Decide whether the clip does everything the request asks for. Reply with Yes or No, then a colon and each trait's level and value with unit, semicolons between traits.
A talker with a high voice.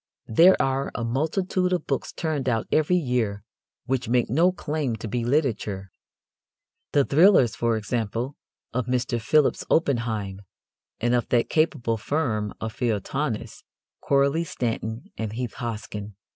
No: low, 125 Hz